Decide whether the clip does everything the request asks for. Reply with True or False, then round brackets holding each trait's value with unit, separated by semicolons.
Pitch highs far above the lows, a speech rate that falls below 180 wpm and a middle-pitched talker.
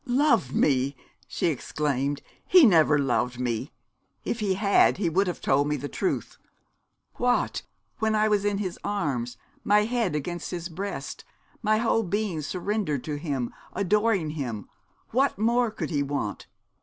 True (6.9 semitones; 155 wpm; 175 Hz)